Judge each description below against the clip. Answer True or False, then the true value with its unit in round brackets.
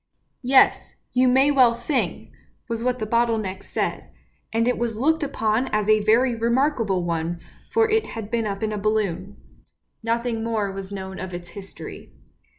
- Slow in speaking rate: False (180 wpm)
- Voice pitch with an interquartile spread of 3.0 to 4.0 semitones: True (3.7 semitones)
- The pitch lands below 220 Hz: False (225 Hz)